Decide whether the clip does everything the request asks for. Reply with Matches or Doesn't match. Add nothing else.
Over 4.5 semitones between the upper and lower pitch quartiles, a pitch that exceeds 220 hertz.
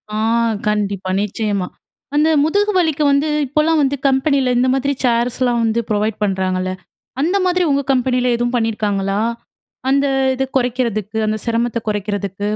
Matches